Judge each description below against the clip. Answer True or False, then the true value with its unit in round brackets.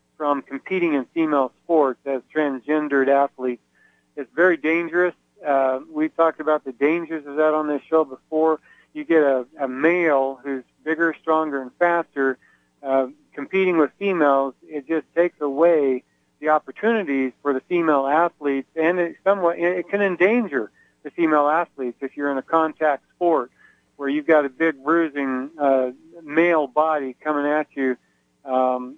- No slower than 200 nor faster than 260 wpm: False (155 wpm)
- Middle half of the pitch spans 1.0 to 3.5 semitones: True (3.2 semitones)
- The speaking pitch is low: False (150 Hz)